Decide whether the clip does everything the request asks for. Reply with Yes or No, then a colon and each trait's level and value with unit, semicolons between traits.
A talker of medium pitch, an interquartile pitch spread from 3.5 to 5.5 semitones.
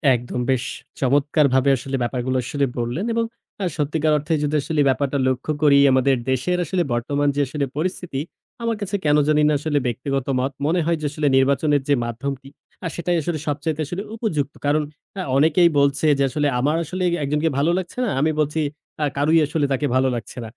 No: medium, 145 Hz; average, 2.7 semitones